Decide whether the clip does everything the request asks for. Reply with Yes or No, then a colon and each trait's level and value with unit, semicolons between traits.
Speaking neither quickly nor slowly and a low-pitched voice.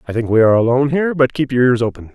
No: fast, 305 wpm; low, 130 Hz